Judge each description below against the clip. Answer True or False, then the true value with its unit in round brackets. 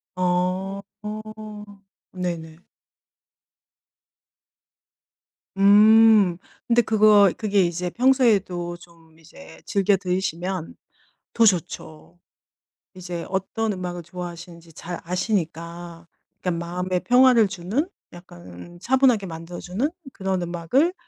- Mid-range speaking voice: True (180 Hz)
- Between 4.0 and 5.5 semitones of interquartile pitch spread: False (3.2 semitones)